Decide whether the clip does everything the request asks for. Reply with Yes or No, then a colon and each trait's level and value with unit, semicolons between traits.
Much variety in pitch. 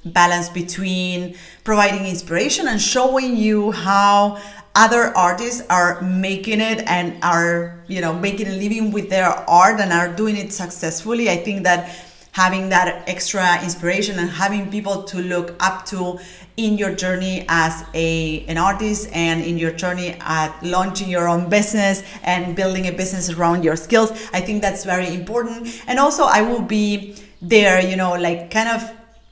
No: average, 2.9 semitones